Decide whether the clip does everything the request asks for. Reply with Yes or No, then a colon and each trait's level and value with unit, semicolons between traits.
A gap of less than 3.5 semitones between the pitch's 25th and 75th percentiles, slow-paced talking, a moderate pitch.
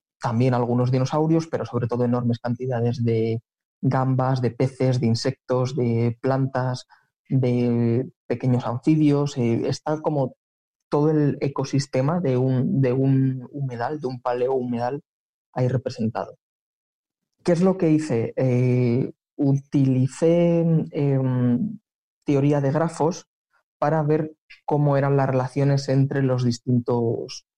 No: average, 2.9 semitones; slow, 120 wpm; low, 130 Hz